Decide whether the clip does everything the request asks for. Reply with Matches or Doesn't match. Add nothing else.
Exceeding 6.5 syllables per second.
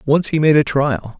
Doesn't match